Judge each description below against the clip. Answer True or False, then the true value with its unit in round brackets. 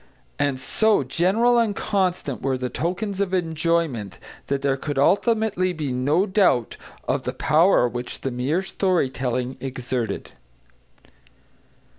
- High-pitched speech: False (155 Hz)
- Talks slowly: True (130 wpm)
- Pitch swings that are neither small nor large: False (6.6 semitones)